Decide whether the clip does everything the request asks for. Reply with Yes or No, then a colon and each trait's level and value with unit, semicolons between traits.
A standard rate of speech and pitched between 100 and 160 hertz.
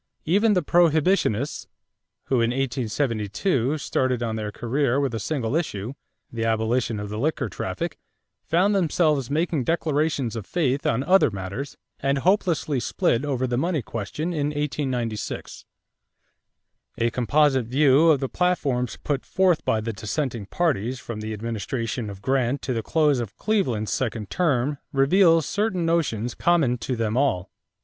Yes: average, 150 wpm; low, 135 Hz